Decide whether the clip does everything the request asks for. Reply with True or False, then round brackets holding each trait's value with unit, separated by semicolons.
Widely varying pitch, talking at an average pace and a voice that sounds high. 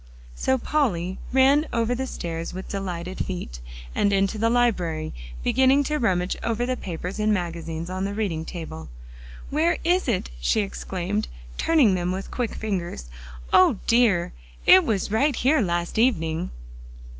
True (5.8 semitones; 150 wpm; 195 Hz)